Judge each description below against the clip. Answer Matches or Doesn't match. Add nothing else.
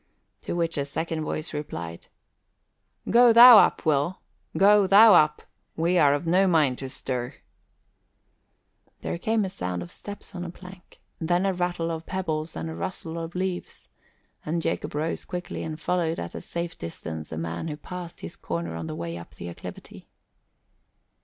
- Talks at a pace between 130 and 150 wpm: Doesn't match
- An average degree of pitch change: Doesn't match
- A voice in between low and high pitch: Matches